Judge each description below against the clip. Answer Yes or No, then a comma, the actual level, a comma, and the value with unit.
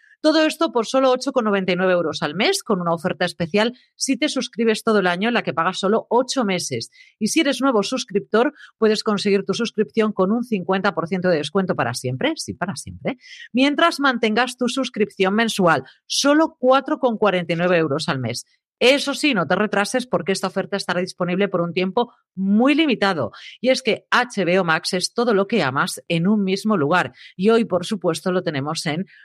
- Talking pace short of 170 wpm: No, average, 185 wpm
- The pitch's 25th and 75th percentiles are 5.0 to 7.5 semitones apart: Yes, wide, 5.5 semitones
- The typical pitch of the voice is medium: No, high, 205 Hz